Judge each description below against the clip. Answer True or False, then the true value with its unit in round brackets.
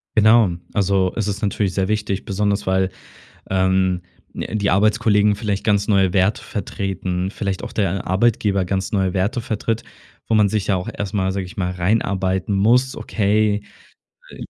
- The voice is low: True (100 Hz)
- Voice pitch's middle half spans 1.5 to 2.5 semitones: True (2.0 semitones)